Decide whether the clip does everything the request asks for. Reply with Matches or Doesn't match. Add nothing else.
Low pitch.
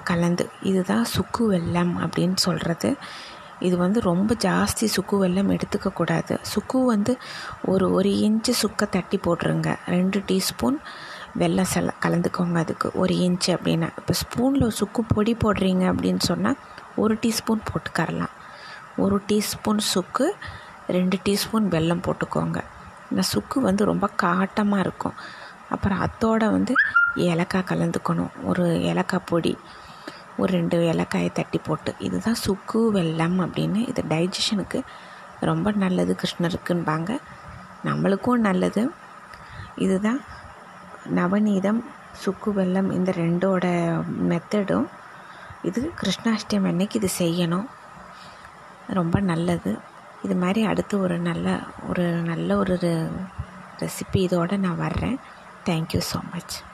Doesn't match